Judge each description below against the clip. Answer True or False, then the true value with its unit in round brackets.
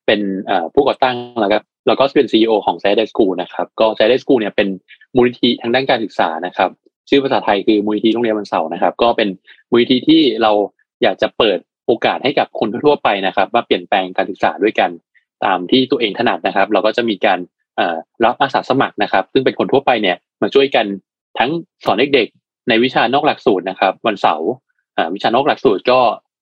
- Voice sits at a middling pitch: False (110 Hz)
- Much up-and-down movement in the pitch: False (3.4 semitones)